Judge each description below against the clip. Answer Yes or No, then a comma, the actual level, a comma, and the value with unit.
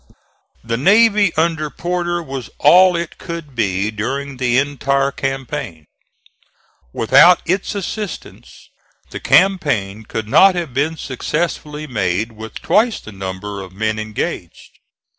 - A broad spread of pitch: Yes, wide, 7.8 semitones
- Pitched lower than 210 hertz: Yes, medium, 140 Hz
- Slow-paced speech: Yes, slow, 120 wpm